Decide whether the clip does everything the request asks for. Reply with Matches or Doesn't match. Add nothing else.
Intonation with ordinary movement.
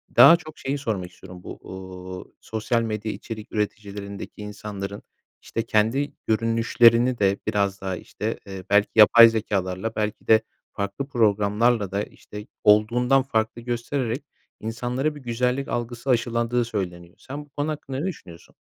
Matches